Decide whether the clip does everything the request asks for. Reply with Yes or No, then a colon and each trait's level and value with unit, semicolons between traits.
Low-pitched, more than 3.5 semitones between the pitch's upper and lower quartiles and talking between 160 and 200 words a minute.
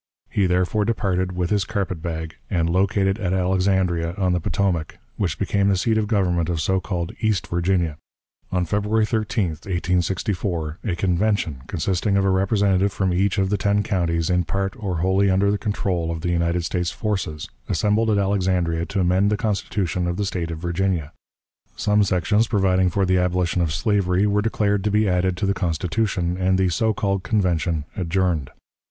No: very low, 95 Hz; narrow, 2.5 semitones; average, 180 wpm